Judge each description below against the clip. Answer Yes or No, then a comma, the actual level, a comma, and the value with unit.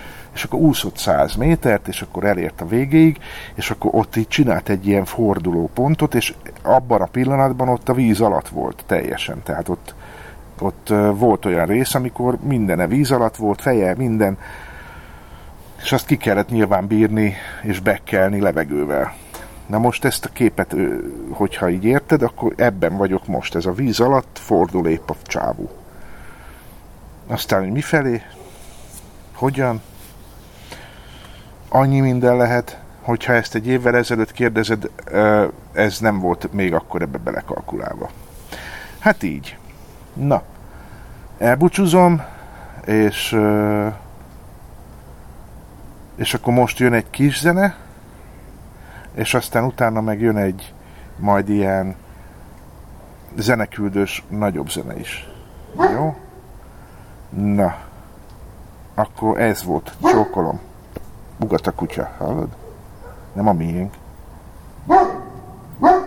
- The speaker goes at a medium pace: Yes, average, 115 wpm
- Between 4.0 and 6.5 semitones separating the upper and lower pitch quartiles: Yes, average, 4.7 semitones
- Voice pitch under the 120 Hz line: Yes, low, 110 Hz